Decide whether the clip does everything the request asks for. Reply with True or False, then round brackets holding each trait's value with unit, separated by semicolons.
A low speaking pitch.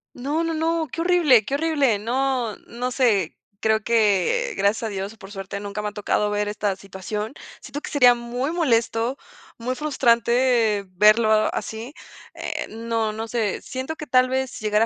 False (235 Hz)